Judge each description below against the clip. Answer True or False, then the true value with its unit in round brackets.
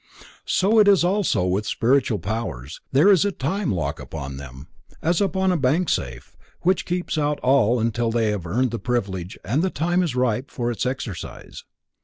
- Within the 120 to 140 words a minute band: False (185 wpm)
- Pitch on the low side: True (125 Hz)